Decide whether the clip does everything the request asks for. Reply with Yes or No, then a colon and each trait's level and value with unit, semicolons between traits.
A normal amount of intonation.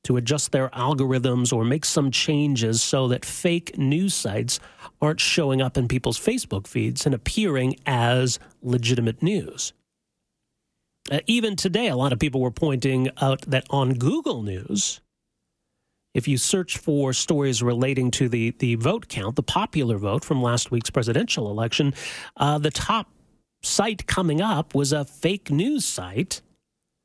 Yes: average, 3.6 semitones